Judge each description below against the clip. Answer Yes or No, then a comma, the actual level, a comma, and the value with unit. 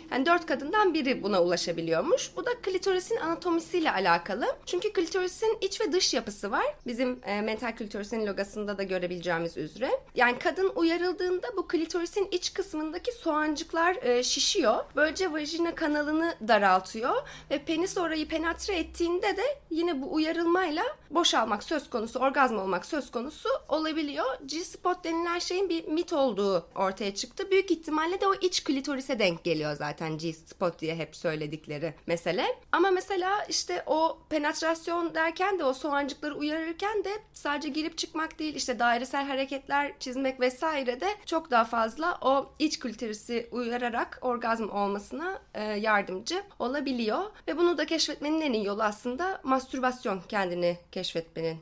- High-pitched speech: Yes, very high, 295 Hz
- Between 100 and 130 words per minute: No, fast, 140 wpm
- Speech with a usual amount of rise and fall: No, wide, 7.5 semitones